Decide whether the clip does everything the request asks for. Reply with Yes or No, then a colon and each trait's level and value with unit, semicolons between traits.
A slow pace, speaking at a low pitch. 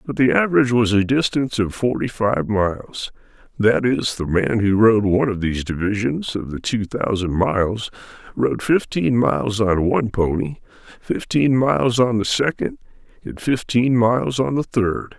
No: average, 165 wpm; low, 110 Hz